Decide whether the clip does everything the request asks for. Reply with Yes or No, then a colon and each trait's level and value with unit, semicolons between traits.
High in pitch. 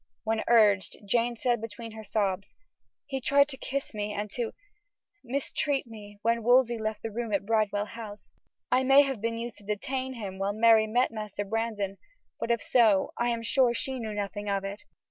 Yes: high, 225 Hz